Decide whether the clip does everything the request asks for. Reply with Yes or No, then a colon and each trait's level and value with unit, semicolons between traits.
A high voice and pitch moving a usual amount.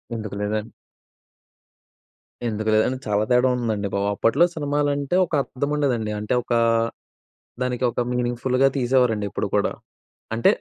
No: low, 120 Hz; average, 3.6 semitones